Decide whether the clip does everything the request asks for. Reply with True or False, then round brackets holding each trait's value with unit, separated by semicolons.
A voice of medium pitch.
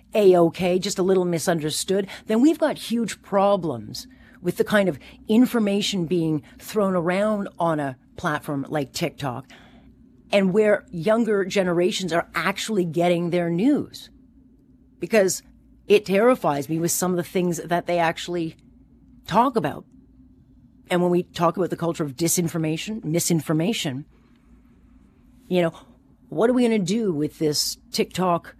True (180 Hz)